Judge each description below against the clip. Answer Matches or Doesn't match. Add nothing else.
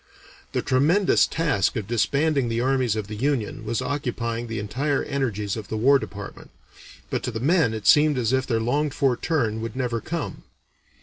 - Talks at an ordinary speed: Matches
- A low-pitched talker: Matches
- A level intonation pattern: Doesn't match